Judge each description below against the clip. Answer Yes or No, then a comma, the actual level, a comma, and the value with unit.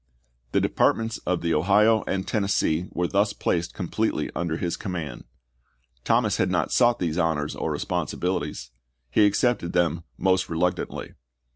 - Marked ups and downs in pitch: No, average, 3.5 semitones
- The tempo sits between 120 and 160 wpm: Yes, average, 140 wpm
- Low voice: Yes, very low, 90 Hz